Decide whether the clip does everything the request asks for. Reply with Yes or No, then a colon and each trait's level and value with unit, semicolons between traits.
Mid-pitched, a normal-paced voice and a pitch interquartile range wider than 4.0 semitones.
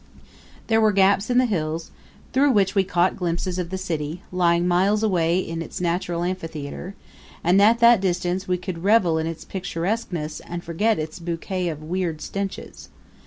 No: medium, 180 Hz; average, 170 wpm; average, 2.9 semitones